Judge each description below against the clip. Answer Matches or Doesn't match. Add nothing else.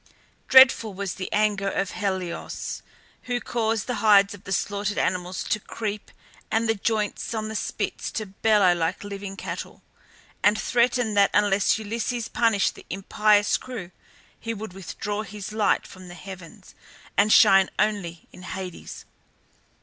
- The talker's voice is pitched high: Matches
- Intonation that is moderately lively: Doesn't match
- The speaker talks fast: Doesn't match